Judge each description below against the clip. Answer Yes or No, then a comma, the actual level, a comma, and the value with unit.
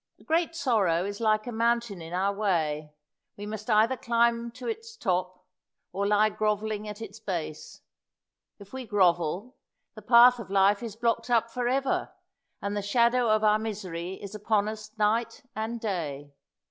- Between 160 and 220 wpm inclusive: Yes, average, 170 wpm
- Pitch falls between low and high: No, high, 215 Hz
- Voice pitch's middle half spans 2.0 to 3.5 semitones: Yes, average, 3.2 semitones